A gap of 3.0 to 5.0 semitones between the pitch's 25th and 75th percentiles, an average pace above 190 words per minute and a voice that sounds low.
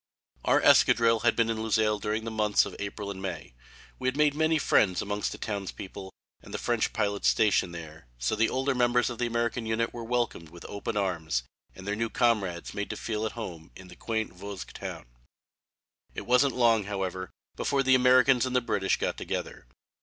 Yes: average, 3.6 semitones; average, 200 wpm; low, 110 Hz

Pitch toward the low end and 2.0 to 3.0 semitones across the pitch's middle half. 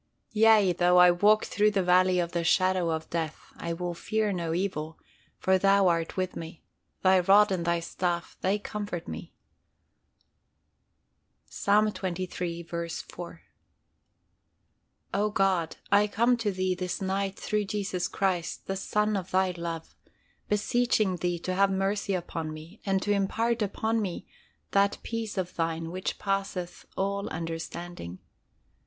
No: medium, 185 Hz; average, 2.7 semitones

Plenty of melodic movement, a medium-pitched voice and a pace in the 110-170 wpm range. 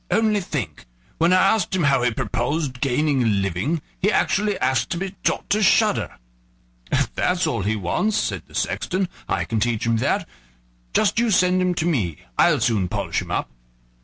No: wide, 8.4 semitones; medium, 150 Hz; average, 190 wpm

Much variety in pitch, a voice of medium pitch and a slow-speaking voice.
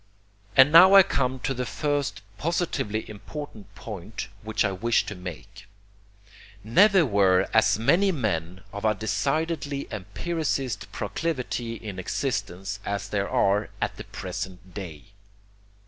No: wide, 6.3 semitones; low, 110 Hz; slow, 130 wpm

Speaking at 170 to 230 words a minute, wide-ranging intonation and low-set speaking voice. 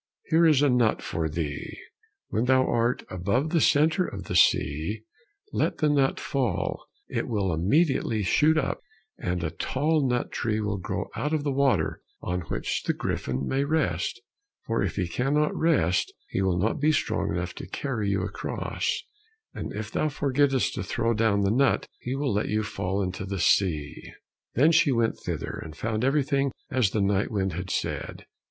Yes: average, 180 wpm; wide, 6.5 semitones; low, 115 Hz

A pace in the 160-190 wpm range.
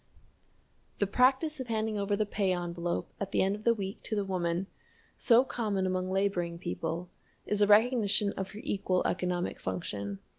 Yes: average, 175 wpm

